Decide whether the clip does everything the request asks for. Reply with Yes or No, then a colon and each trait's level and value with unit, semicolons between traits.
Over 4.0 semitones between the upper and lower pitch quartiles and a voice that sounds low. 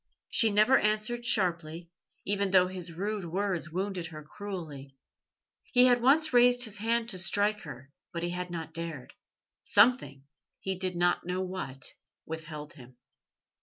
No: average, 4.5 semitones; medium, 185 Hz